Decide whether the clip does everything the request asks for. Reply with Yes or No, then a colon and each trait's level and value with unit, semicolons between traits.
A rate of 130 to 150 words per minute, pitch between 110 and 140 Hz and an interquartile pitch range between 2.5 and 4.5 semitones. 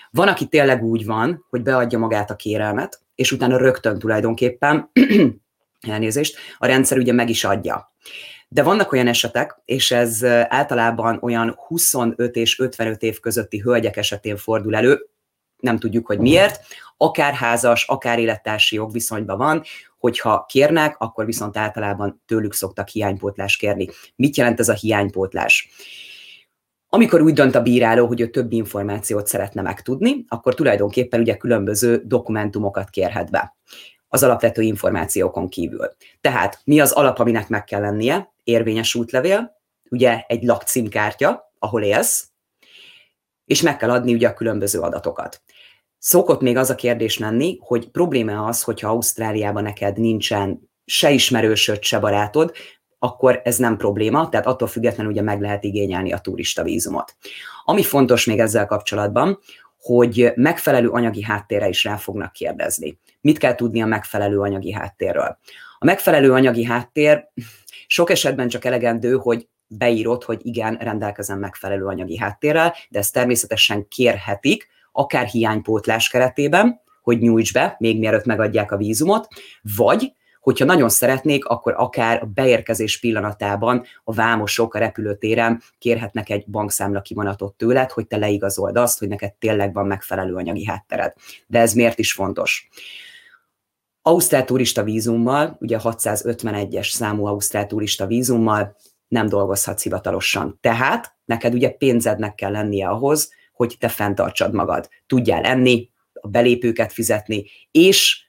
Yes: average, 140 wpm; low, 115 Hz; average, 2.9 semitones